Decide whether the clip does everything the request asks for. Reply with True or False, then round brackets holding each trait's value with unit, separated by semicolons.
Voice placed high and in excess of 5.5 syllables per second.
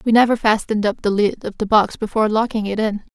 True (215 Hz; 6.4 syllables/s)